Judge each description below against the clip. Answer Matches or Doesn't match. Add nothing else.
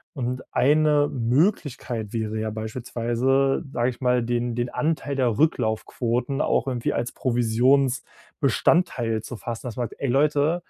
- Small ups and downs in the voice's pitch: Doesn't match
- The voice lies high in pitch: Doesn't match